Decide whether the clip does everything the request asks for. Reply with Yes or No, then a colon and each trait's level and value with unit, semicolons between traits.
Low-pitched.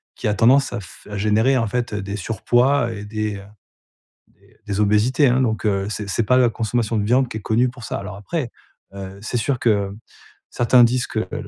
Yes: low, 110 Hz